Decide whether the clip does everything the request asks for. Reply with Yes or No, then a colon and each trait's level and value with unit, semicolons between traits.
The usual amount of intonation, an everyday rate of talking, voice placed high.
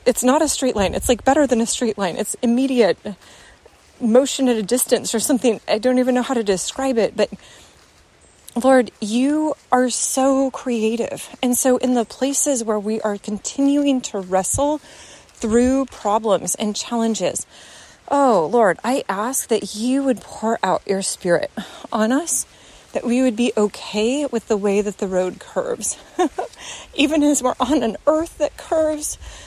Yes: average, 3.9 semitones; average, 165 wpm; high, 245 Hz